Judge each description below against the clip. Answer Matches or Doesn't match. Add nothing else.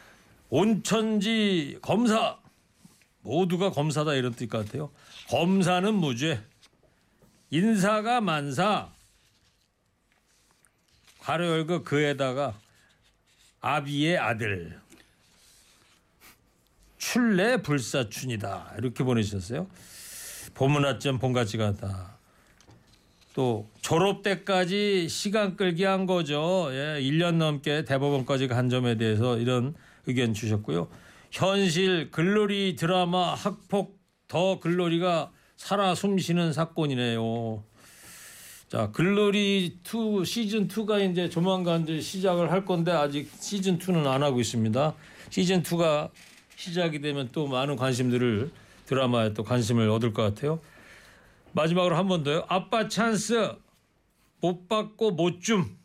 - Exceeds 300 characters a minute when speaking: Doesn't match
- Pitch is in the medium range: Matches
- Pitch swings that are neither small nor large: Doesn't match